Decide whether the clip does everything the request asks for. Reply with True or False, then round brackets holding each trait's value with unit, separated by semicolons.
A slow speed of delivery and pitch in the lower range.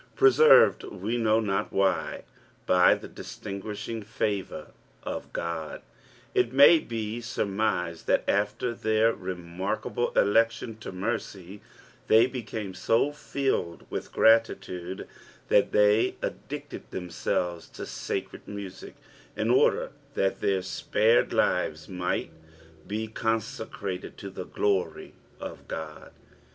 True (110 wpm; 105 Hz)